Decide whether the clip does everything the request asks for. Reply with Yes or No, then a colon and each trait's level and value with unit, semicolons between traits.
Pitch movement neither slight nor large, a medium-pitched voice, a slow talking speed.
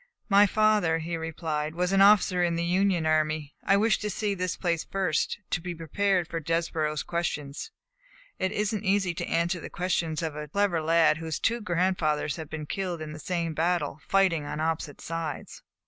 No: average, 3.2 semitones; medium, 170 Hz; average, 190 wpm